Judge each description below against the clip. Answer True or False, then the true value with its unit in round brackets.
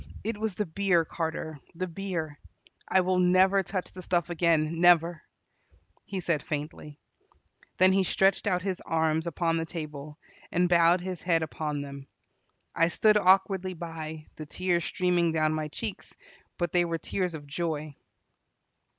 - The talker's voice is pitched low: False (170 Hz)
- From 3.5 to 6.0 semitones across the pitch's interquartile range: False (2.7 semitones)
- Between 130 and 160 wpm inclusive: True (155 wpm)